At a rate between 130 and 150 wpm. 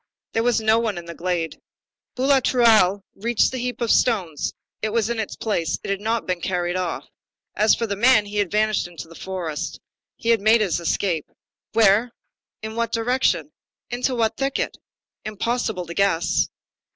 No: average, 175 wpm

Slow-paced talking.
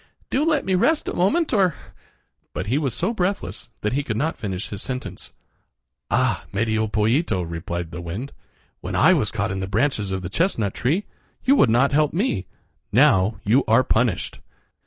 No: average, 180 wpm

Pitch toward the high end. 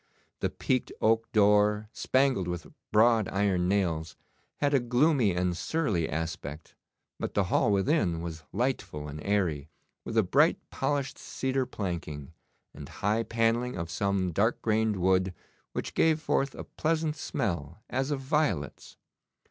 No: low, 105 Hz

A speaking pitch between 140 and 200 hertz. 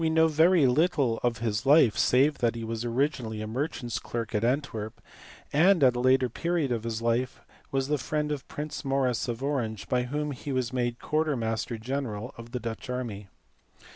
No: low, 125 Hz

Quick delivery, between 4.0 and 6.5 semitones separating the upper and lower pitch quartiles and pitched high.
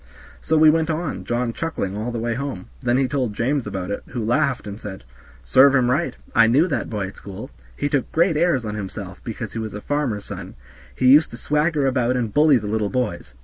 No: fast, 230 wpm; average, 5.3 semitones; low, 125 Hz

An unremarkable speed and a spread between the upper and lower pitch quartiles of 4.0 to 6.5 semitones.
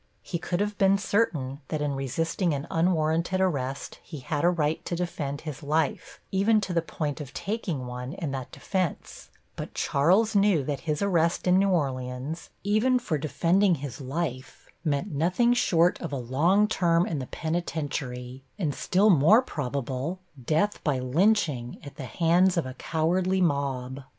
Yes: average, 165 wpm; average, 5.0 semitones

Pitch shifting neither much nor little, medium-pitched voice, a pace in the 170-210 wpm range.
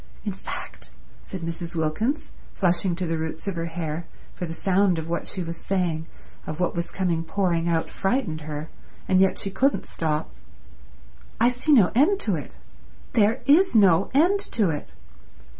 Yes: average, 4.1 semitones; medium, 180 Hz; average, 175 wpm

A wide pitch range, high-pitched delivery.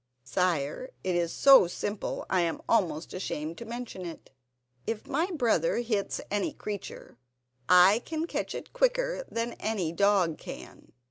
Yes: wide, 5.7 semitones; high, 200 Hz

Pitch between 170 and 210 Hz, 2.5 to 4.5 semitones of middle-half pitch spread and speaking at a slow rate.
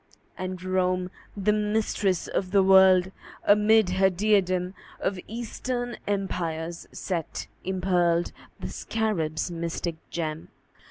Yes: medium, 185 Hz; average, 2.8 semitones; slow, 105 wpm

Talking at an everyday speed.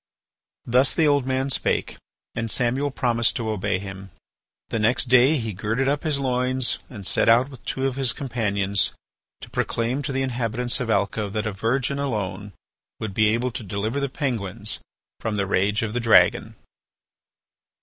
Yes: average, 175 wpm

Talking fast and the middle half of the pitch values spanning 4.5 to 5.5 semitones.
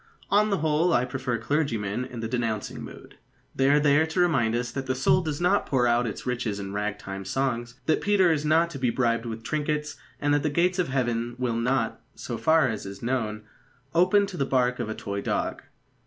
Yes: fast, 220 wpm; average, 4.9 semitones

